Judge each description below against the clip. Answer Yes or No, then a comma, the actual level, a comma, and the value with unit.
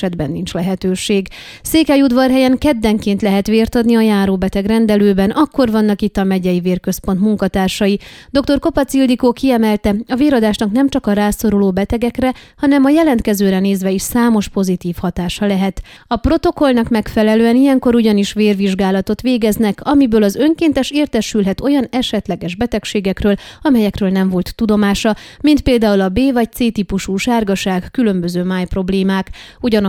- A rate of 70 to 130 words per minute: No, average, 140 wpm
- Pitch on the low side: No, high, 215 Hz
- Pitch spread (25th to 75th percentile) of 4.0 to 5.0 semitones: Yes, average, 4.4 semitones